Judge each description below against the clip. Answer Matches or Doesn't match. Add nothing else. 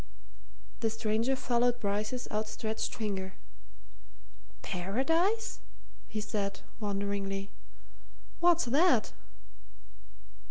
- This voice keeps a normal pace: Doesn't match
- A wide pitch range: Doesn't match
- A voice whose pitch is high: Matches